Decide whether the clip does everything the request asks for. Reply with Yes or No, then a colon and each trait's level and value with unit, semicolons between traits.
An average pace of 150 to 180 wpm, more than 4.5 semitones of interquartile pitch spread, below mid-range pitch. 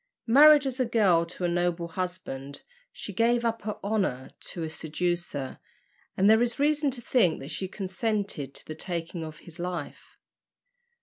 No: average, 170 wpm; wide, 5.5 semitones; medium, 185 Hz